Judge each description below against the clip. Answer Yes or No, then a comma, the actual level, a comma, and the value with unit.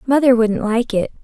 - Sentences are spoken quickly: No, average, 195 wpm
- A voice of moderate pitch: No, high, 235 Hz